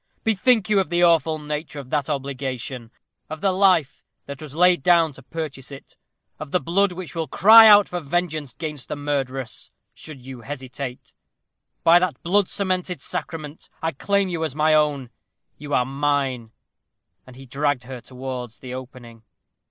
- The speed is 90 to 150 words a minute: No, average, 165 wpm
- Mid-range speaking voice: Yes, medium, 150 Hz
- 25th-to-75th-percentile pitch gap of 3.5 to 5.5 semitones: Yes, average, 4.7 semitones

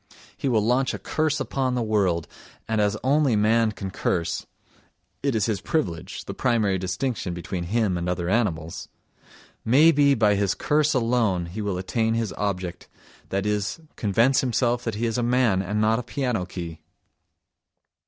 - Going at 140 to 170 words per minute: Yes, average, 165 wpm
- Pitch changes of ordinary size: Yes, average, 4.6 semitones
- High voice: No, low, 110 Hz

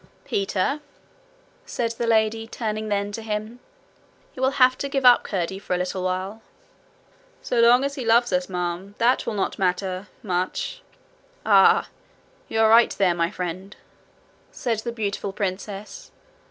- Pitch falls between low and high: No, high, 210 Hz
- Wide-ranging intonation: No, average, 3.7 semitones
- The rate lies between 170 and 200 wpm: No, average, 155 wpm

